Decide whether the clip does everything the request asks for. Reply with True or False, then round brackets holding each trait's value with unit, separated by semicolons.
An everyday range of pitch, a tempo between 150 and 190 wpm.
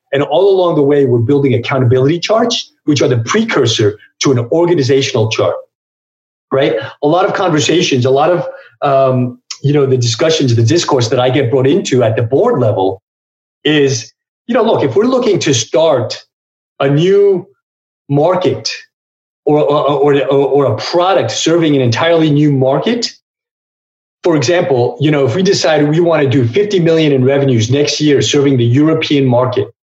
True (4.5 semitones; 170 wpm)